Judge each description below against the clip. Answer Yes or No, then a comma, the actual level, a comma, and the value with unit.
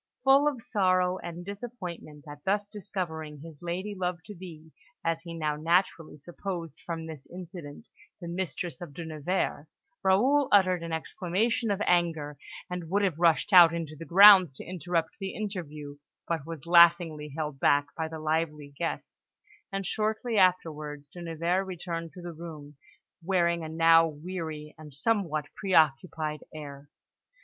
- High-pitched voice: No, medium, 170 Hz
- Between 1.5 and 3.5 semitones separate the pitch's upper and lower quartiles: Yes, average, 3.2 semitones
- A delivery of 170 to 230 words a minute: No, average, 155 wpm